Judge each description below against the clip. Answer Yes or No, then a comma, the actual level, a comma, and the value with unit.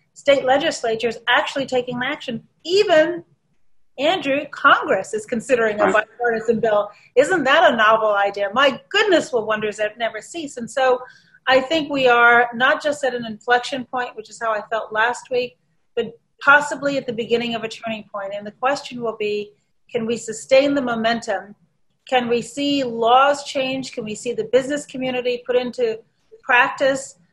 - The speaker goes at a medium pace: Yes, average, 170 wpm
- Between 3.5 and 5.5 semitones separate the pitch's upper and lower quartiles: Yes, average, 3.8 semitones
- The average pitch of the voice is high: Yes, high, 245 Hz